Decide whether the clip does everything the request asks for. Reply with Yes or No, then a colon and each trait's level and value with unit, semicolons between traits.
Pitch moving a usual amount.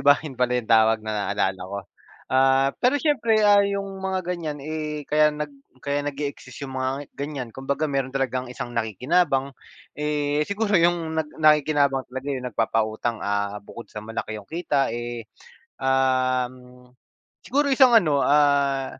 Yes: average, 3.6 semitones